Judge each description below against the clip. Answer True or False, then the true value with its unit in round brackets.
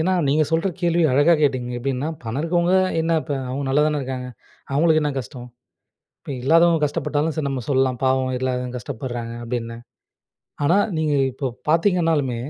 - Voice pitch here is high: False (140 Hz)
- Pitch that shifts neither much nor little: True (4.1 semitones)